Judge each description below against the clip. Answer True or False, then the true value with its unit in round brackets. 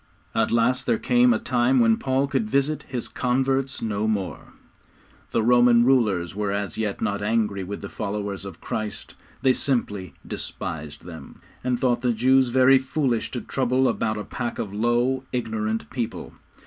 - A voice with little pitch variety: False (3.6 semitones)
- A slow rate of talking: False (165 wpm)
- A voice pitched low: True (120 Hz)